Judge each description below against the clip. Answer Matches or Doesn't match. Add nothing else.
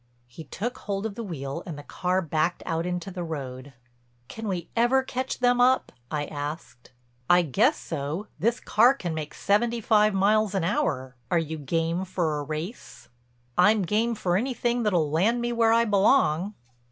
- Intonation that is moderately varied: Doesn't match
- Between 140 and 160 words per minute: Doesn't match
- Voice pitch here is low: Doesn't match